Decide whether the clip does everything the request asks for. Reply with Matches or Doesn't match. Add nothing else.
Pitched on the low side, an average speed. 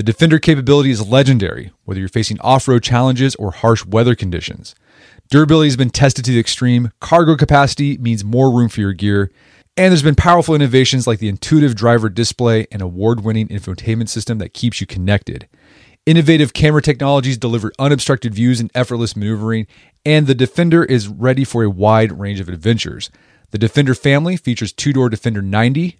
Matches